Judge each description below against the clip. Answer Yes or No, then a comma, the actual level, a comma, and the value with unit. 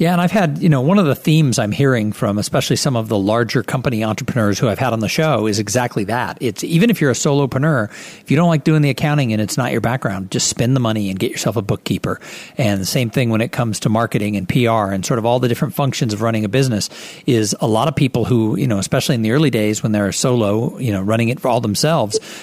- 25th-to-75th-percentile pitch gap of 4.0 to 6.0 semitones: Yes, average, 5.0 semitones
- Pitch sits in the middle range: No, low, 125 Hz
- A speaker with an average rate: No, fast, 270 wpm